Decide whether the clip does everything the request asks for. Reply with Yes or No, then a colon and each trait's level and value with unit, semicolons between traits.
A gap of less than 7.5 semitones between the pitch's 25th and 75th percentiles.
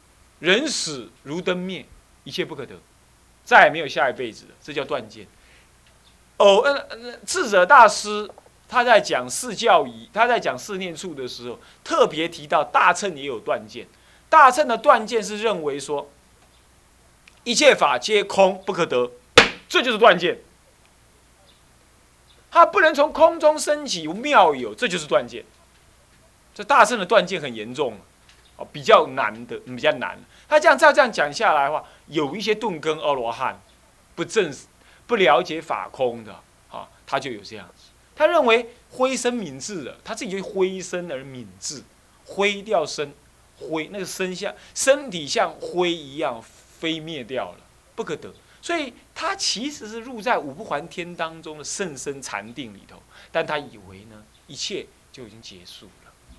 No: wide, 9.0 semitones